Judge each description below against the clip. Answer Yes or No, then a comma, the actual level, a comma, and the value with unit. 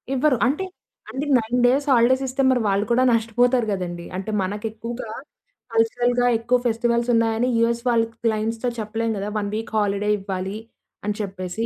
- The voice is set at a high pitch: Yes, high, 230 Hz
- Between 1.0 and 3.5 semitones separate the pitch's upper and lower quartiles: Yes, average, 2.7 semitones